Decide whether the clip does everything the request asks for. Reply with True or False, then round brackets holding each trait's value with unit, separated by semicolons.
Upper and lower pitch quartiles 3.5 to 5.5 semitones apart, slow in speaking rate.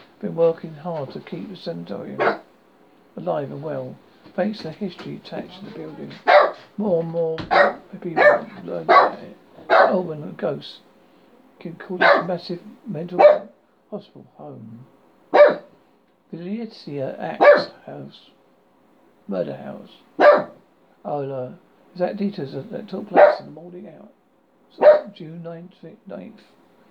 True (3.9 semitones; 125 wpm)